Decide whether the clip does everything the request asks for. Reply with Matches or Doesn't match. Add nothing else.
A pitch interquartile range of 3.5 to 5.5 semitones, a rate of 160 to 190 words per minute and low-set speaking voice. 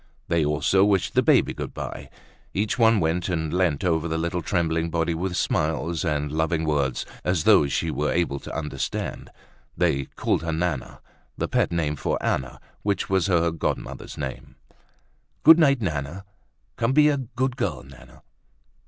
Matches